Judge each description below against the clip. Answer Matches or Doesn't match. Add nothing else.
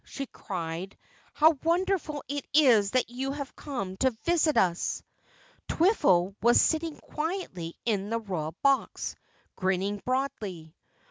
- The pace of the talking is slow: Matches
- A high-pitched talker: Matches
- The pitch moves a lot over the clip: Matches